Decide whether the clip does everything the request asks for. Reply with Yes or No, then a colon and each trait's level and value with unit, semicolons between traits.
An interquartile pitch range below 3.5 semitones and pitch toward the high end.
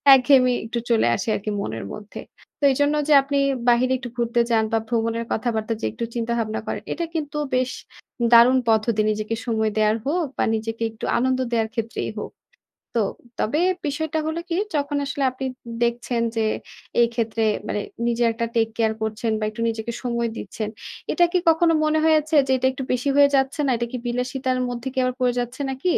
Yes: average, 3.1 semitones; high, 240 Hz